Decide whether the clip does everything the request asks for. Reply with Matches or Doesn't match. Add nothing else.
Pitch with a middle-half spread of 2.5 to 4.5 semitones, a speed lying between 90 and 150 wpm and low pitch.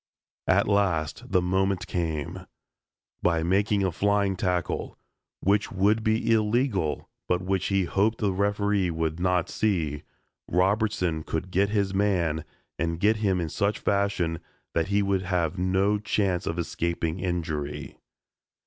Matches